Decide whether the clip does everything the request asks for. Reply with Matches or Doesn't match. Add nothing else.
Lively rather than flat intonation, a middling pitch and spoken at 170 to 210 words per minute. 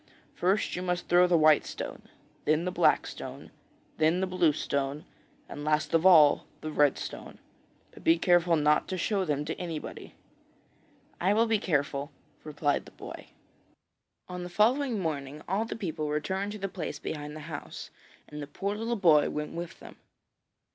Doesn't match